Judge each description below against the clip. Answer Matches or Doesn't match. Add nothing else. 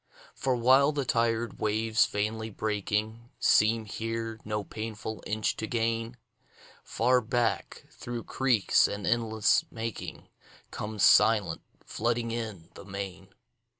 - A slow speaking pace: Matches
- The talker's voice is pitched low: Matches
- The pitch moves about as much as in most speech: Doesn't match